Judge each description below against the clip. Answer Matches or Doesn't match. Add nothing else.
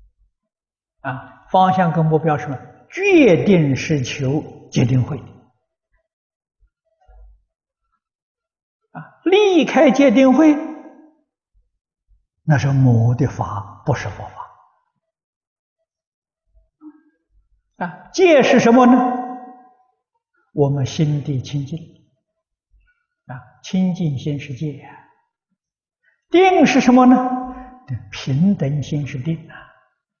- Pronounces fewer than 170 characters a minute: Matches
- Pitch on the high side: Matches